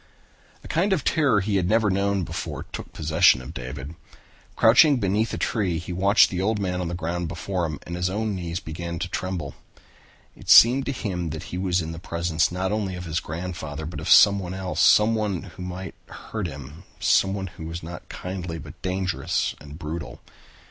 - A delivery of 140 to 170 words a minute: No, average, 190 wpm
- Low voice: Yes, very low, 90 Hz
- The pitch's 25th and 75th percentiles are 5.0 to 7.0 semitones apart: No, average, 3.0 semitones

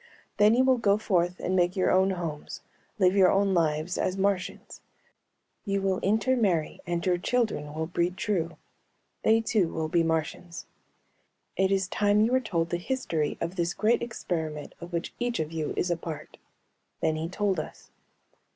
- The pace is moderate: Yes, average, 175 wpm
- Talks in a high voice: No, medium, 180 Hz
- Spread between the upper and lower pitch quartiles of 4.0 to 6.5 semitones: No, average, 3.6 semitones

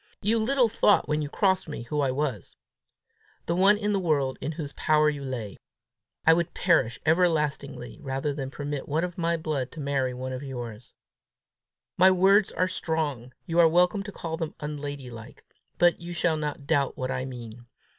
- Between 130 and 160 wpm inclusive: No, average, 185 wpm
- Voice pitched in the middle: Yes, medium, 150 Hz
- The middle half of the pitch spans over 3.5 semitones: Yes, average, 4.5 semitones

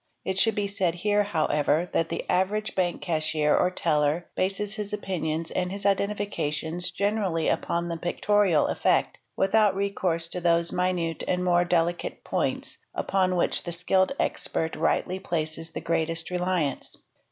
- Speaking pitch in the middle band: Yes, medium, 180 Hz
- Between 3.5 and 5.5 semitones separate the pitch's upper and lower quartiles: No, average, 2.9 semitones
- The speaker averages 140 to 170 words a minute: Yes, average, 150 wpm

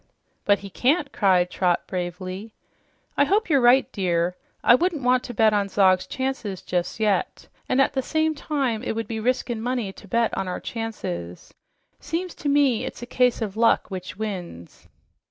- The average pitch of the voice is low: No, high, 225 Hz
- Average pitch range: No, wide, 5.7 semitones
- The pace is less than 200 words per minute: Yes, average, 180 wpm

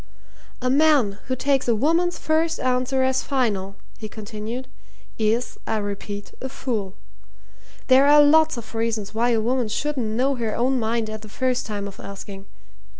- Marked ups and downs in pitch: No, average, 3.8 semitones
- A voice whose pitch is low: No, high, 235 Hz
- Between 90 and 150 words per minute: No, average, 165 wpm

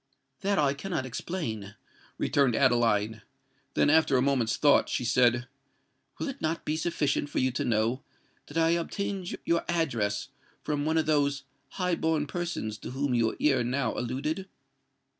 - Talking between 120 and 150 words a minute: No, average, 160 wpm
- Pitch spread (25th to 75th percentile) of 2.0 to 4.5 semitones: No, average, 5.0 semitones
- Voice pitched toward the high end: No, medium, 140 Hz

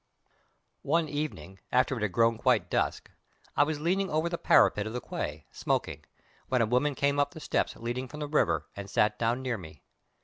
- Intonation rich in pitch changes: Yes, wide, 5.7 semitones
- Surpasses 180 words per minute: Yes, average, 200 wpm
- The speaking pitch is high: No, low, 125 Hz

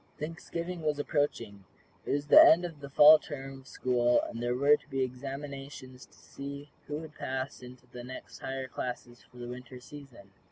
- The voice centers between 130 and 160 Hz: Yes, low, 135 Hz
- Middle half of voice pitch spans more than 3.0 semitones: No, average, 2.7 semitones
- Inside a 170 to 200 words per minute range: Yes, average, 190 wpm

